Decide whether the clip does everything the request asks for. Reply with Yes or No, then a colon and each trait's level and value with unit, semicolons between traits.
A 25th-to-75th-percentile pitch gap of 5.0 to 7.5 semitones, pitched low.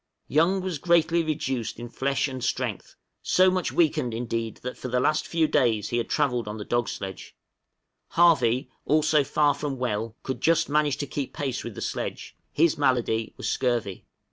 No: average, 4.5 semitones; low, 130 Hz